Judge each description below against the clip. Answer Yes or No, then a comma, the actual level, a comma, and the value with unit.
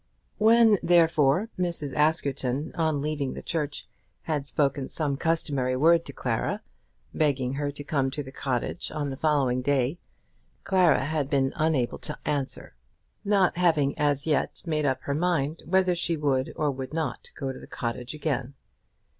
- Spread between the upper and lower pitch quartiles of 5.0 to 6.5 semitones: No, average, 3.1 semitones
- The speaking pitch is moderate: Yes, medium, 145 Hz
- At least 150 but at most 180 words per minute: Yes, average, 160 wpm